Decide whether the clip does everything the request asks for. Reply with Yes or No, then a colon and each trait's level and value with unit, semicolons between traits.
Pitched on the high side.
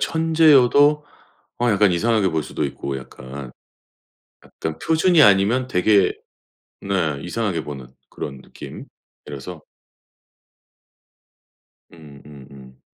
No: very low, 90 Hz